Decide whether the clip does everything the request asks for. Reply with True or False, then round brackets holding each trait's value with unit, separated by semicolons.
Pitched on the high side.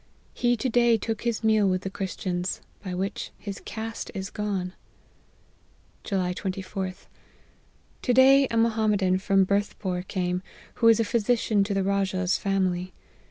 True (200 Hz)